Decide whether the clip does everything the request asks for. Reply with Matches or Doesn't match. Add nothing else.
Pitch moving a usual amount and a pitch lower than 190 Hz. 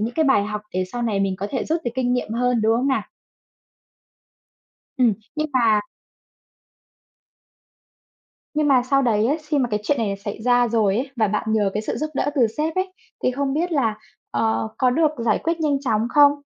Doesn't match